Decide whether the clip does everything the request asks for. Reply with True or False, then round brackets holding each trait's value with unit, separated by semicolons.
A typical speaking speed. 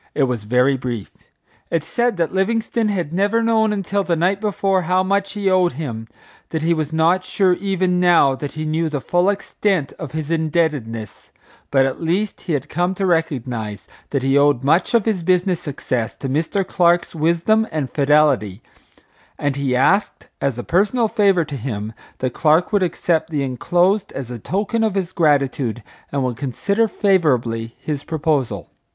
True (175 wpm)